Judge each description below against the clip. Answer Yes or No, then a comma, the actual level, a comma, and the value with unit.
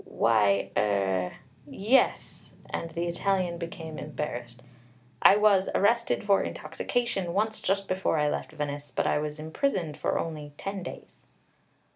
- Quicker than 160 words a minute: No, slow, 135 wpm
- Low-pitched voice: No, medium, 165 Hz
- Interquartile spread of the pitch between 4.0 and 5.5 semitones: Yes, average, 5.0 semitones